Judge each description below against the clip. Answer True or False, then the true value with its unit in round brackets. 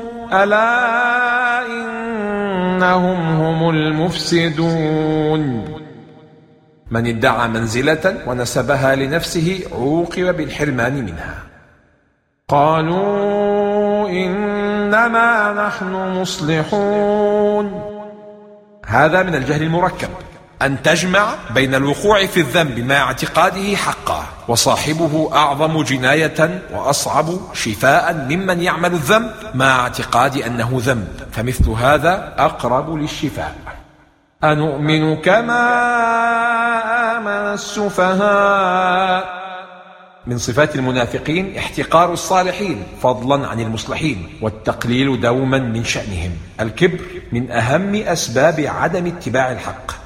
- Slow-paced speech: True (80 wpm)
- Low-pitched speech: False (165 Hz)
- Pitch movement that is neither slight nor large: False (7.2 semitones)